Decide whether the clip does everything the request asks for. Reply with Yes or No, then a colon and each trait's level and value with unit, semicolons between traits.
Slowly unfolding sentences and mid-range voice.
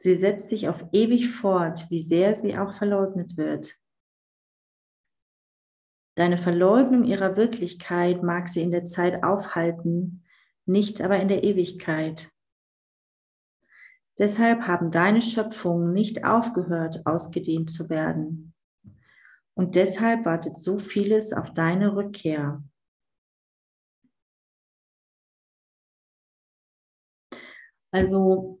Yes: slow, 95 wpm; medium, 180 Hz